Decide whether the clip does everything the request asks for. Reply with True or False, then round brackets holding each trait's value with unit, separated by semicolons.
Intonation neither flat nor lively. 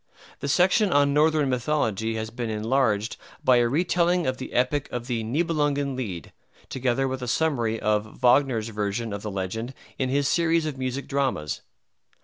True (4.3 semitones)